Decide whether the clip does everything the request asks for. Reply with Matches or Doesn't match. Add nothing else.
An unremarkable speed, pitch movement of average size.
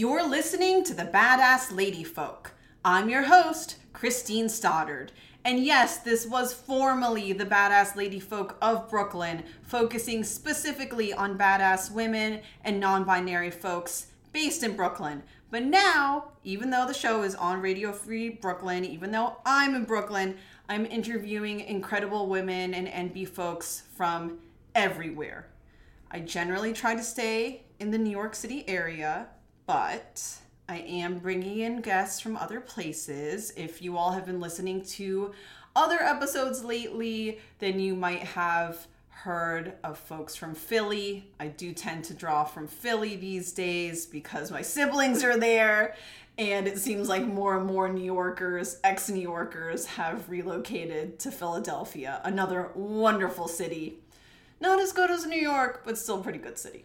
Matches